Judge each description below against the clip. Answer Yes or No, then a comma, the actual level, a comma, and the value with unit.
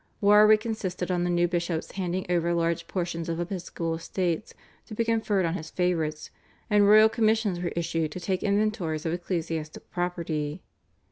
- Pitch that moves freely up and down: No, average, 3.3 semitones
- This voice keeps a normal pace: Yes, average, 160 wpm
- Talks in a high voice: No, medium, 175 Hz